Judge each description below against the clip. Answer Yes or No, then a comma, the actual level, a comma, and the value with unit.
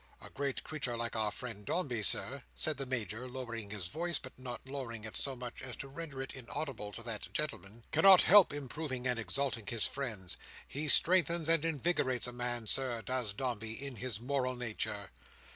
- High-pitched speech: No, low, 125 Hz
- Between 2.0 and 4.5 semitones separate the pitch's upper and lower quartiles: Yes, average, 3.7 semitones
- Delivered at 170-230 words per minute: Yes, average, 185 wpm